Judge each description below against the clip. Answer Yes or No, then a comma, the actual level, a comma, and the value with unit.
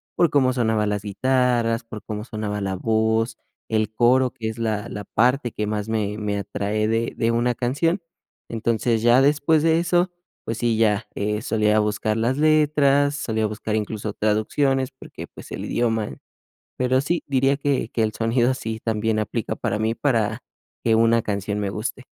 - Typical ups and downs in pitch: Yes, average, 3.2 semitones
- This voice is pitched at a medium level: No, low, 115 Hz